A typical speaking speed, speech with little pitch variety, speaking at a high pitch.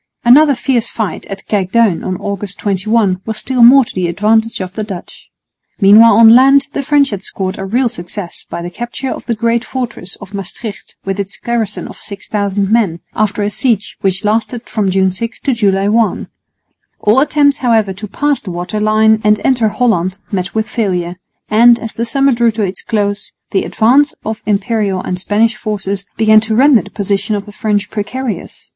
No: average, 190 wpm; average, 3.0 semitones; high, 215 Hz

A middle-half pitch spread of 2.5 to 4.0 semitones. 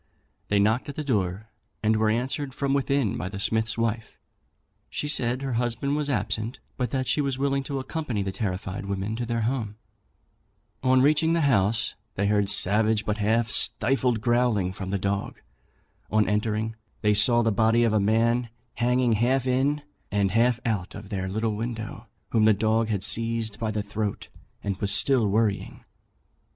Yes: average, 3.2 semitones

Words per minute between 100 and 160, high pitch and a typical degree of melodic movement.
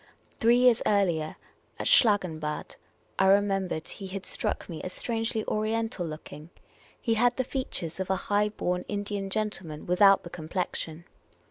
Yes: average, 150 wpm; high, 195 Hz; average, 3.8 semitones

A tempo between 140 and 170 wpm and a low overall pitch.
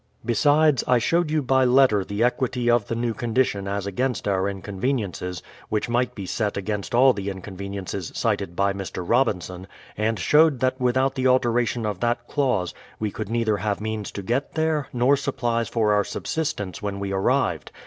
No: average, 180 wpm; low, 115 Hz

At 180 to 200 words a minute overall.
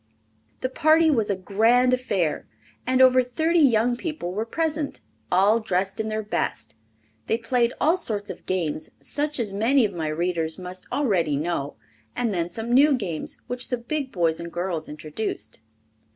No: average, 165 wpm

